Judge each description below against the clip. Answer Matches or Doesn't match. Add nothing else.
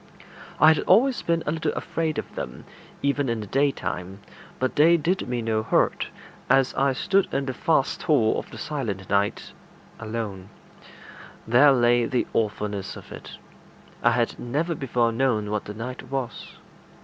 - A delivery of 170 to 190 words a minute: Doesn't match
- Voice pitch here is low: Matches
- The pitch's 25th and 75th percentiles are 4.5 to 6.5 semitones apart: Matches